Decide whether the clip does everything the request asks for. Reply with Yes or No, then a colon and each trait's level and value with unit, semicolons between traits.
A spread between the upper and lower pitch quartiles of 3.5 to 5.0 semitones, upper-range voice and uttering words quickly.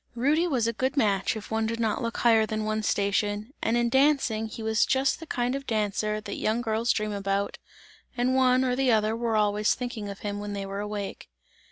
No: average, 2.9 semitones; high, 220 Hz; fast, 220 wpm